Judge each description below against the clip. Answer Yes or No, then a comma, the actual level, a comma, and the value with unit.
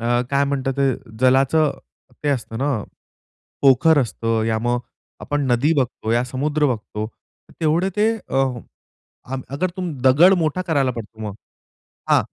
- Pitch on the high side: No, low, 135 Hz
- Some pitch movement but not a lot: Yes, average, 3.9 semitones